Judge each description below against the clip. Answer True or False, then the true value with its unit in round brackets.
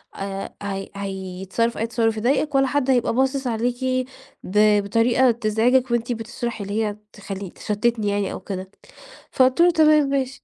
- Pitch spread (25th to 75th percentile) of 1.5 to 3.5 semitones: False (4.1 semitones)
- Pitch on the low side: False (230 Hz)